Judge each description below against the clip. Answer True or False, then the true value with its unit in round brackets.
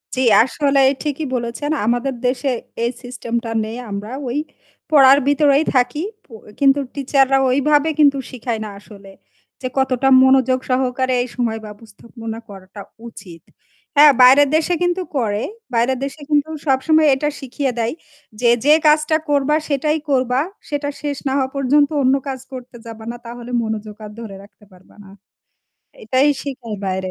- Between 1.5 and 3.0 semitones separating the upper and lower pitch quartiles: False (3.6 semitones)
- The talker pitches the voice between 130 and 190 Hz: False (260 Hz)